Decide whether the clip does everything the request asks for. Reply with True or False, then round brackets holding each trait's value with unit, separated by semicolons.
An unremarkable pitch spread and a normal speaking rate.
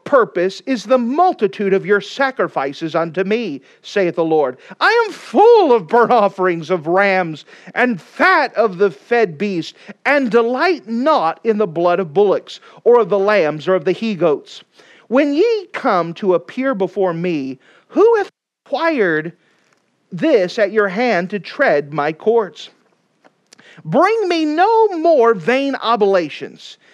False (7.8 semitones; 150 wpm)